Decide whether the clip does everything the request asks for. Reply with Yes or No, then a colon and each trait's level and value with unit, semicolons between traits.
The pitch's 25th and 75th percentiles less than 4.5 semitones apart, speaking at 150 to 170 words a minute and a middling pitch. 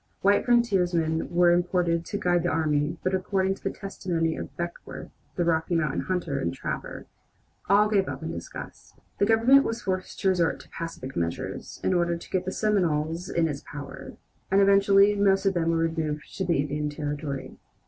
No: average, 3.3 semitones; average, 185 wpm; medium, 175 Hz